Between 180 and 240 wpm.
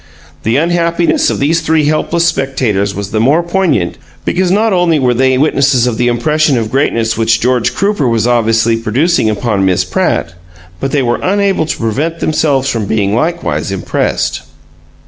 No: average, 165 wpm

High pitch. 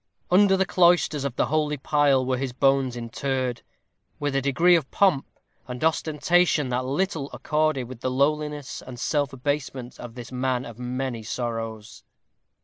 No: low, 135 Hz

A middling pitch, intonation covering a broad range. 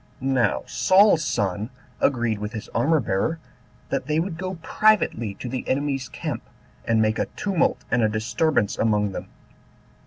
No: low, 125 Hz; wide, 6.9 semitones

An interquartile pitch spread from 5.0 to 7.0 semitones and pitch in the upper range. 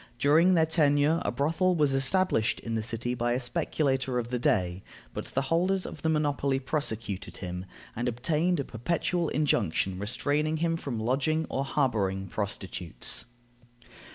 No: wide, 5.6 semitones; low, 135 Hz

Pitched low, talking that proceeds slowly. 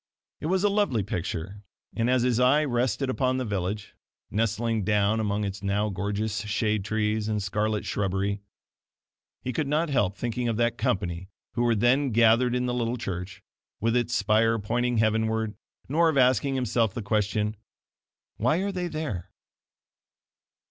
No: low, 110 Hz; average, 160 wpm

